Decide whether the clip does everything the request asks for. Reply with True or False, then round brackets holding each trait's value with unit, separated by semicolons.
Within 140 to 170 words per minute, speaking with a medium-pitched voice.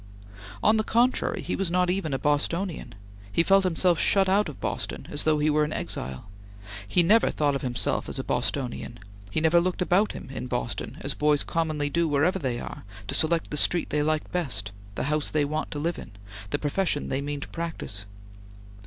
False (205 wpm; 155 Hz)